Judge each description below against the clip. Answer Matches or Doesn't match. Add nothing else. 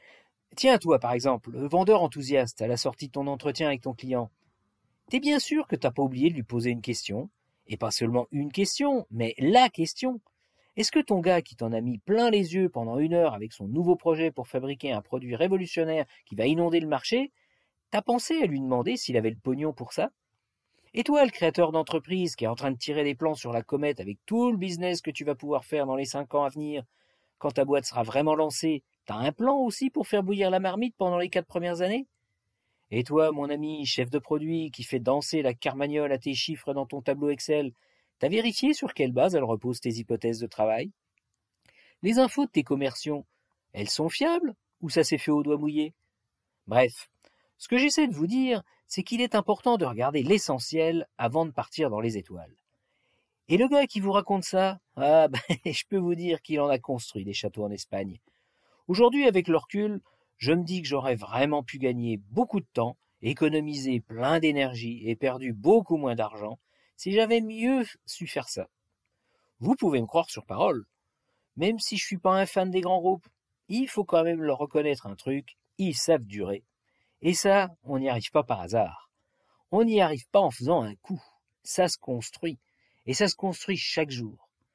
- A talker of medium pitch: Matches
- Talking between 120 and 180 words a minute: Doesn't match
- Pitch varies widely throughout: Matches